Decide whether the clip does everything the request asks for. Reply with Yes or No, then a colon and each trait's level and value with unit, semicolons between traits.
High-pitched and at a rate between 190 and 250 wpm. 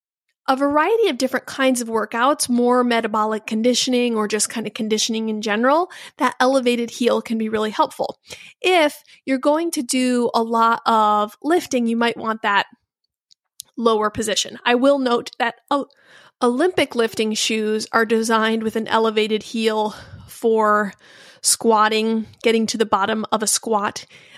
No: high, 230 Hz; average, 150 wpm